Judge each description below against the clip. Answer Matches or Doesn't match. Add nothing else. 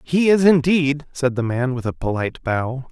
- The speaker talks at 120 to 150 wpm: Doesn't match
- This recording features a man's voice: Matches